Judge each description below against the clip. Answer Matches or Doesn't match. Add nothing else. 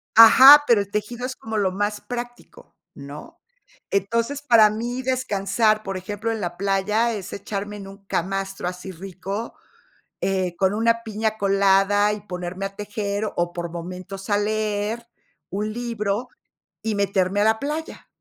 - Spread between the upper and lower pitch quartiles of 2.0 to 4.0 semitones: Matches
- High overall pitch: Matches